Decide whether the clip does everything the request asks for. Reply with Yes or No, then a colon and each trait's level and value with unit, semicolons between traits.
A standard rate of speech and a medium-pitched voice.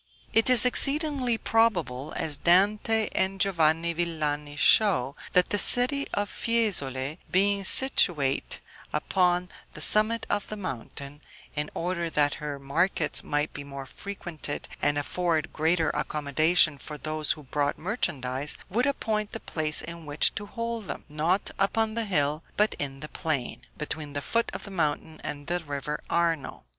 Yes: average, 150 wpm; medium, 165 Hz